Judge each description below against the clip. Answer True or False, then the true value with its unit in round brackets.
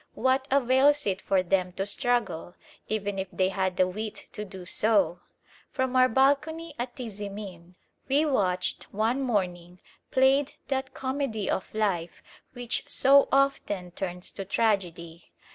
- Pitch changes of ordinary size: False (6.0 semitones)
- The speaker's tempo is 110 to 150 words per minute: True (140 wpm)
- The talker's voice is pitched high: True (210 Hz)